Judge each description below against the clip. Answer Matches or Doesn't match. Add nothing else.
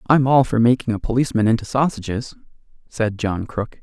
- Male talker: Matches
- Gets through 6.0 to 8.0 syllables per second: Doesn't match